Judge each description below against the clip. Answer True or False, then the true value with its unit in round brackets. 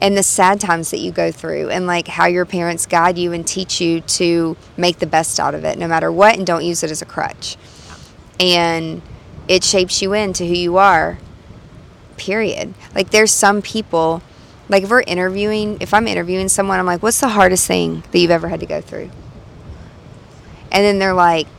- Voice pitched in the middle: True (180 Hz)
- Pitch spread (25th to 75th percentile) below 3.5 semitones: True (2.7 semitones)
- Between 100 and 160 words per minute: False (205 wpm)